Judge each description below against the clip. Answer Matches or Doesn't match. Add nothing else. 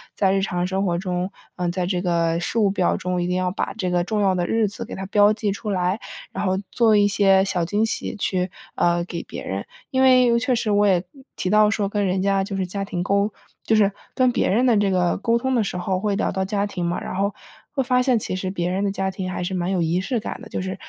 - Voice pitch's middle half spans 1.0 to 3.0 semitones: Matches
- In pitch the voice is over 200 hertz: Doesn't match